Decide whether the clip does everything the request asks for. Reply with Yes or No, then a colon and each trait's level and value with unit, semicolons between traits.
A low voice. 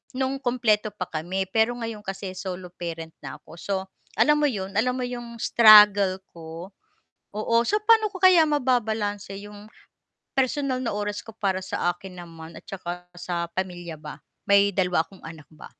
No: high, 200 Hz